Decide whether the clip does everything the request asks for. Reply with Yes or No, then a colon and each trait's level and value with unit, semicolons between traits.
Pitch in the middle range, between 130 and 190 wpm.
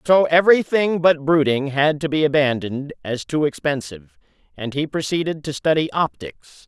Yes: medium, 150 Hz; average, 155 wpm